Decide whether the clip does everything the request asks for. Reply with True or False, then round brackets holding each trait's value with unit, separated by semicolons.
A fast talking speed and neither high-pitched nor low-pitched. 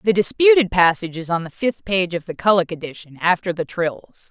True (210 wpm; 180 Hz)